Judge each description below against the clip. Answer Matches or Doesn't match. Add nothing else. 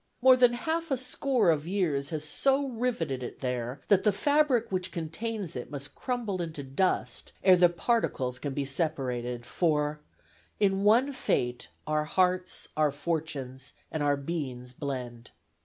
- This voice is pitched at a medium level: Matches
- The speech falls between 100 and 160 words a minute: Matches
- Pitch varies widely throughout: Matches